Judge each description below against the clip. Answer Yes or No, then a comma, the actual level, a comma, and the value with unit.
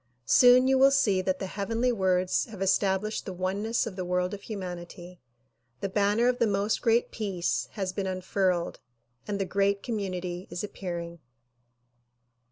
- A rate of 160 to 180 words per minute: Yes, average, 165 wpm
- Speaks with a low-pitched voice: No, high, 195 Hz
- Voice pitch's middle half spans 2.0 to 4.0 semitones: Yes, average, 2.8 semitones